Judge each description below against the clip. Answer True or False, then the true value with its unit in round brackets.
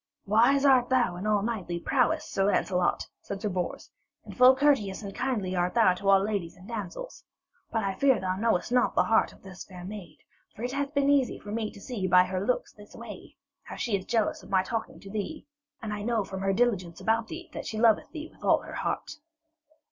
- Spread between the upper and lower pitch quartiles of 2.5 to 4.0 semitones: False (4.4 semitones)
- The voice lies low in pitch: False (210 Hz)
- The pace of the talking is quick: True (225 wpm)